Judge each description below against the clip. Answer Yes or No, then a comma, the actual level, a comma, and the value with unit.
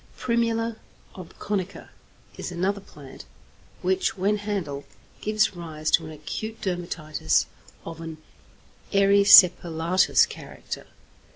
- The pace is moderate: No, slow, 95 wpm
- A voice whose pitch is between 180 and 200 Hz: Yes, medium, 185 Hz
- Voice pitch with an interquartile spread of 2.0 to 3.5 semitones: No, average, 4.2 semitones